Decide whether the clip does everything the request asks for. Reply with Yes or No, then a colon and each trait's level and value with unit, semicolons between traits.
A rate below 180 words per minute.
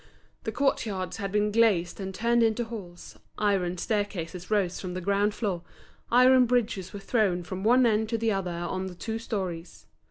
No: average, 185 wpm